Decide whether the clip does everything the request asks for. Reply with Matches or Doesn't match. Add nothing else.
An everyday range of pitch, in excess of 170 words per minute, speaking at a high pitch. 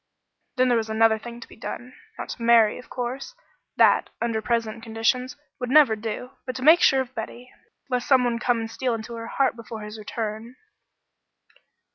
Doesn't match